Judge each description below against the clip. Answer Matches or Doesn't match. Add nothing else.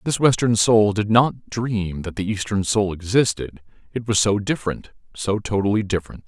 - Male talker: Matches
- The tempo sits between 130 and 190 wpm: Matches